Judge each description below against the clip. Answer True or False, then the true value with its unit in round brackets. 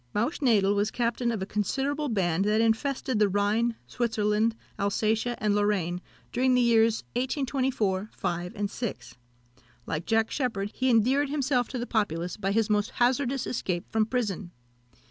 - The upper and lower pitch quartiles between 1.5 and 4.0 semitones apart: True (3.5 semitones)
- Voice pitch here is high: True (220 Hz)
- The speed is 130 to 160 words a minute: True (155 wpm)